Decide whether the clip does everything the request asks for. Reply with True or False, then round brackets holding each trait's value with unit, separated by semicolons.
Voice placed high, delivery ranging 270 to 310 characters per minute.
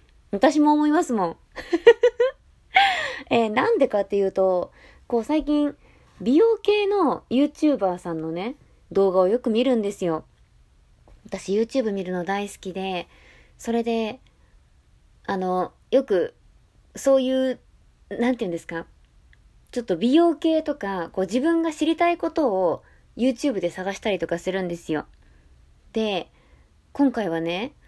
True (230 Hz; 280 characters per minute)